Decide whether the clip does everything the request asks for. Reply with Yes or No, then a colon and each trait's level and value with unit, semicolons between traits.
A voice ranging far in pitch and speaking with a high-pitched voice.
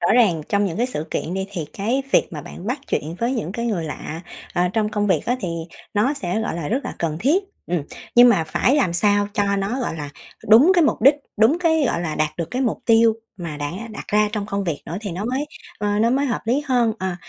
Yes: wide, 5.8 semitones; high, 210 Hz